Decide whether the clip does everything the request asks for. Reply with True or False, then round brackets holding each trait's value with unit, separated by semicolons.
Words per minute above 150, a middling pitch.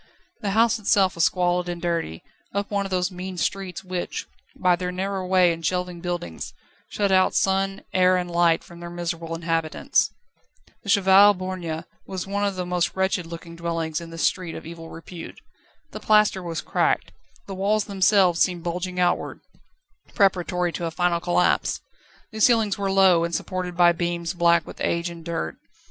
True (175 wpm; 180 Hz)